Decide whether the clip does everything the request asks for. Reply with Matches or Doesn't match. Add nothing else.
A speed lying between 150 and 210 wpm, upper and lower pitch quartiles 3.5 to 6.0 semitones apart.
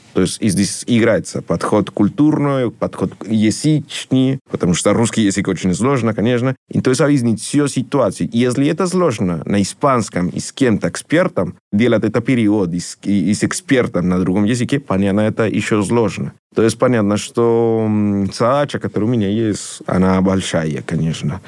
Matches